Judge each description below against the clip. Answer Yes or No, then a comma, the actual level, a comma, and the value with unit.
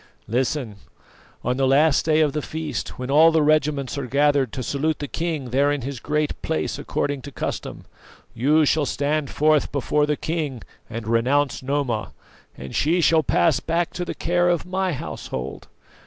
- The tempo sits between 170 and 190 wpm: Yes, average, 175 wpm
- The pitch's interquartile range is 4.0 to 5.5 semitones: No, average, 2.9 semitones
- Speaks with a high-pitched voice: No, medium, 145 Hz